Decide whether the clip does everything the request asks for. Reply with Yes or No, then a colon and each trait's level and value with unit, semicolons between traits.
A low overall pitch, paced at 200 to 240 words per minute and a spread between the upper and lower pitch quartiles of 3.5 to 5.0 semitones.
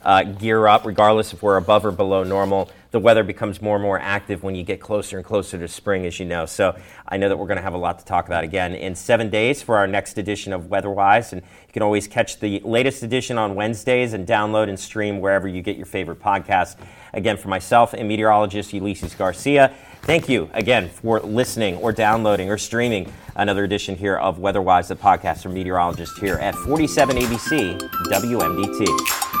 No: low, 100 Hz; fast, 205 wpm; narrow, 2.5 semitones